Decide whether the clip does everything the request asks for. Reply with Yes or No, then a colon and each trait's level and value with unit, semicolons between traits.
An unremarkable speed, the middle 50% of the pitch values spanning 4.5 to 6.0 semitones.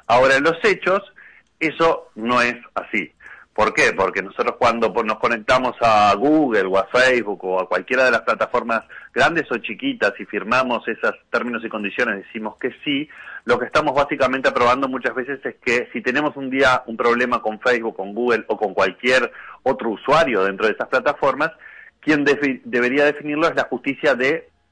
Yes: average, 180 wpm; average, 5.0 semitones